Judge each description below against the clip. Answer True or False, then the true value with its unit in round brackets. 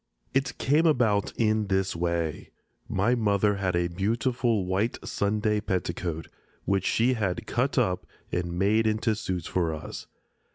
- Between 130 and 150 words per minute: True (140 wpm)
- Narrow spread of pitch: False (3.7 semitones)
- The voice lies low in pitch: True (100 Hz)